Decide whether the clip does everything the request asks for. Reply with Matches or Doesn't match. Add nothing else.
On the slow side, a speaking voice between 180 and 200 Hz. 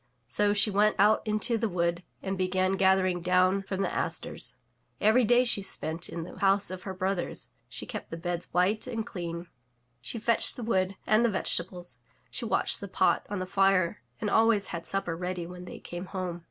Doesn't match